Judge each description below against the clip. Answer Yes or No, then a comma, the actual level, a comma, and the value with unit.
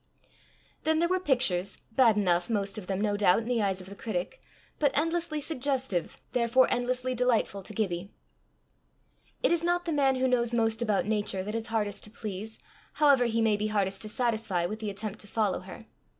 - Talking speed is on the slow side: No, average, 195 wpm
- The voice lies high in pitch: Yes, high, 220 Hz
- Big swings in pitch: No, average, 4.2 semitones